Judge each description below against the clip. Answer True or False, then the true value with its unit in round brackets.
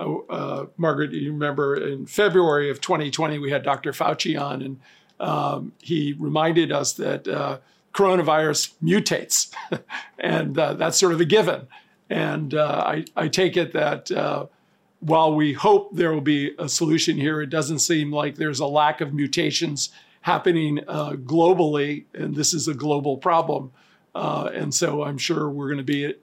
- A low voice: False (155 Hz)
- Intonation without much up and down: True (2.2 semitones)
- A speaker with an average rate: True (165 wpm)